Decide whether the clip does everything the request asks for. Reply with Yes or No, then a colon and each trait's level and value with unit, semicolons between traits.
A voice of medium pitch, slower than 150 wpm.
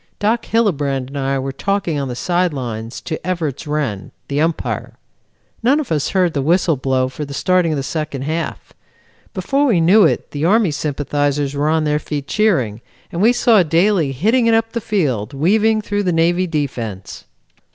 No: medium, 155 Hz; average, 185 wpm